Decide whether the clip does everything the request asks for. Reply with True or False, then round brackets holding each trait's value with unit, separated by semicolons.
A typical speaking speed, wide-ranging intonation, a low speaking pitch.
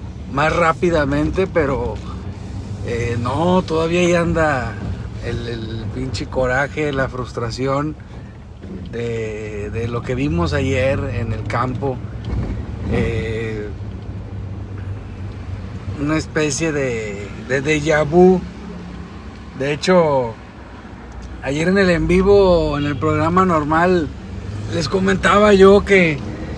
False (100 wpm; 7.3 semitones; 120 Hz)